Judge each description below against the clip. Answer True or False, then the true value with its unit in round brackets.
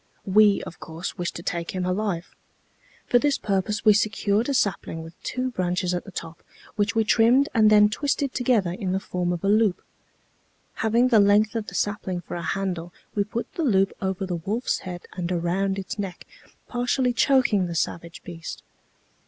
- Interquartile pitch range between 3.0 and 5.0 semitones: True (3.8 semitones)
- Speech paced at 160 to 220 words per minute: True (185 wpm)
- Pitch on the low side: False (200 Hz)